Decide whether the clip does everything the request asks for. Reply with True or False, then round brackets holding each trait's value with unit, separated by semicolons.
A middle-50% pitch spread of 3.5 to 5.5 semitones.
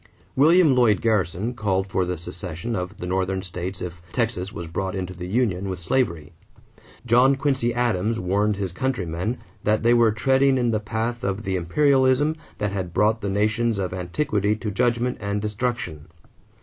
True (4.7 semitones)